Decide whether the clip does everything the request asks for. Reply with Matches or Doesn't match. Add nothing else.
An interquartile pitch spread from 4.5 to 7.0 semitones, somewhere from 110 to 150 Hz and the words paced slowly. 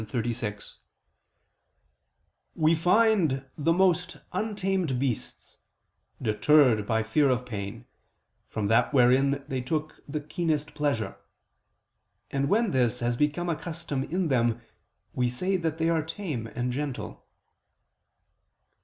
Matches